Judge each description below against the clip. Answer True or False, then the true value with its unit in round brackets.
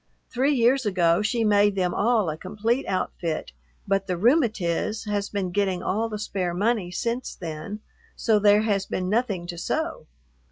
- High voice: True (205 Hz)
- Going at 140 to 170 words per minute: True (165 wpm)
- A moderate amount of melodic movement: True (3.5 semitones)